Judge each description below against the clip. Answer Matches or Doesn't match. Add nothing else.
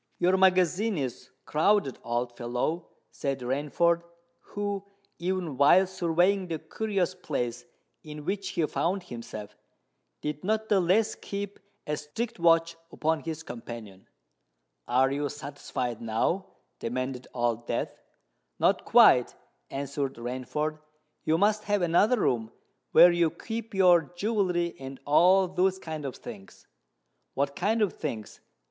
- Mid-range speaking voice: Matches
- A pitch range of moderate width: Doesn't match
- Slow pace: Matches